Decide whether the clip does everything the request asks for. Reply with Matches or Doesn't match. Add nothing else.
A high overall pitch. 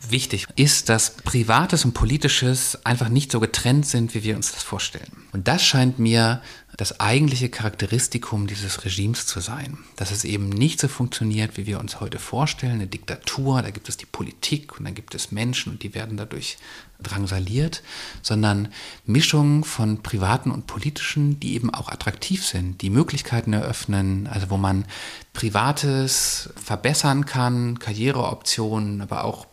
Doesn't match